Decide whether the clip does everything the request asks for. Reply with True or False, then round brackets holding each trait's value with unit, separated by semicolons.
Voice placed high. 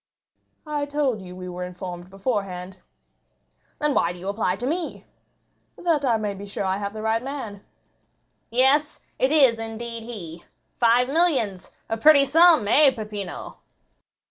True (225 Hz)